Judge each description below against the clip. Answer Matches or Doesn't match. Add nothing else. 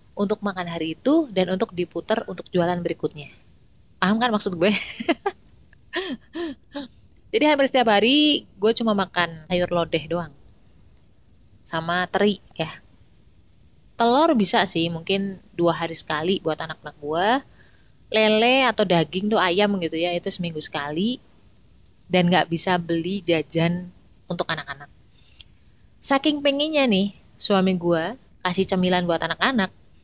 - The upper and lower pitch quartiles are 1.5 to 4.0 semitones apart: Doesn't match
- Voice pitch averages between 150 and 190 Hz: Matches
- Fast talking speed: Doesn't match